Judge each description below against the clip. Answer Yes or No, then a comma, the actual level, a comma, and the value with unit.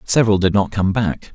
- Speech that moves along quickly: Yes, fast, 225 wpm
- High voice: No, low, 100 Hz